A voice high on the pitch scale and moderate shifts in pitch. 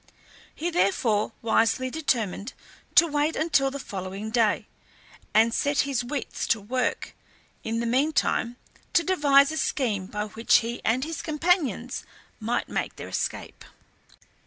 Yes: very high, 250 Hz; average, 4.8 semitones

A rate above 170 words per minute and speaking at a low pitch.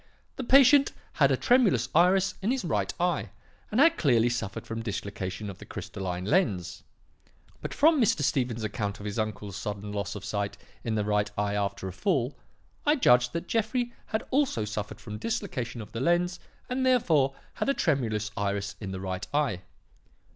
Yes: average, 180 wpm; low, 115 Hz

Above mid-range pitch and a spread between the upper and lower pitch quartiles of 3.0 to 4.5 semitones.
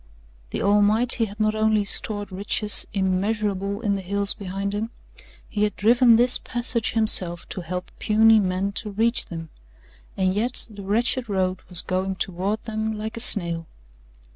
No: high, 205 Hz; narrow, 2.6 semitones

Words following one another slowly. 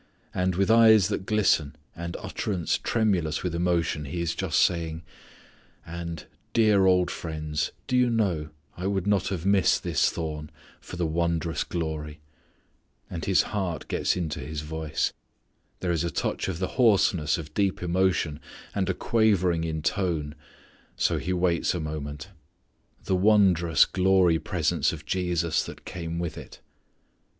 No: average, 150 wpm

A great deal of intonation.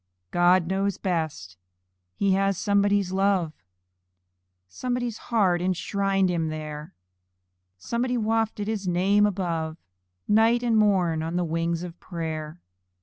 No: average, 3.7 semitones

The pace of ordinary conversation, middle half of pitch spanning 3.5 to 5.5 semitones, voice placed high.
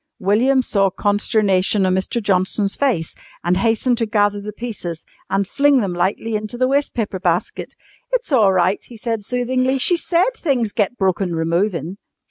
Yes: average, 165 wpm; average, 4.6 semitones; high, 210 Hz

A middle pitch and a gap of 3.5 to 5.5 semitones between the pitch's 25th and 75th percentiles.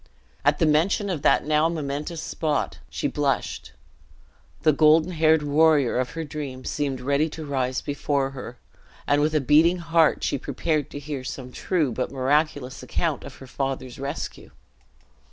No: medium, 145 Hz; average, 2.7 semitones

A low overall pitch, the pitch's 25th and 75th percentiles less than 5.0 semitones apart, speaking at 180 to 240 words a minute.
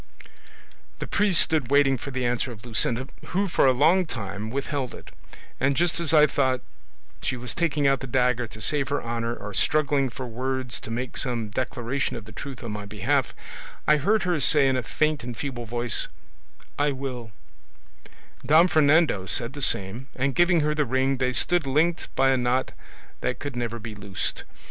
Yes: low, 130 Hz; average, 3.6 semitones; average, 190 wpm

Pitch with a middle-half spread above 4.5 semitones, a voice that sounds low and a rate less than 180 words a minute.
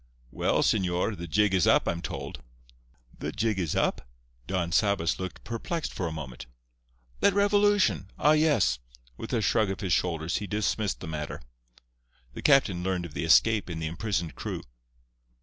Yes: average, 5.0 semitones; very low, 95 Hz; average, 165 wpm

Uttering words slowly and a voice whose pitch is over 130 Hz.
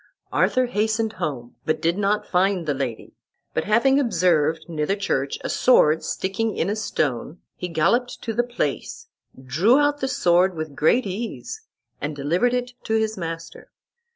No: average, 165 wpm; high, 190 Hz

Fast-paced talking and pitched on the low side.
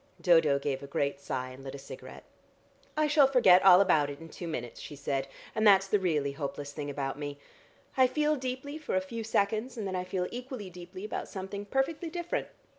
No: fast, 210 wpm; medium, 185 Hz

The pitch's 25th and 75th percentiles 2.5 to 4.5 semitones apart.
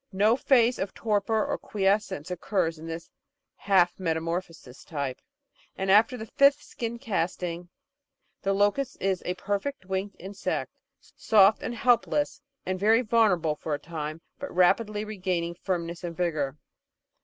Yes: average, 4.2 semitones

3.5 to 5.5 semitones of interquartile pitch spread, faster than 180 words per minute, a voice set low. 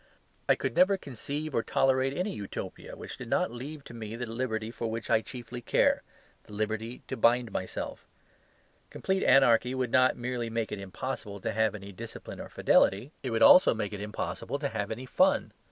No: average, 3.0 semitones; average, 190 wpm; low, 115 Hz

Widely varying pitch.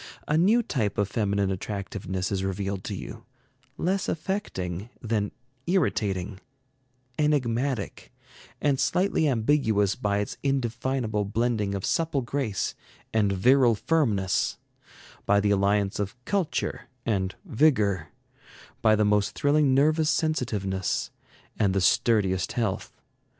Yes: wide, 5.8 semitones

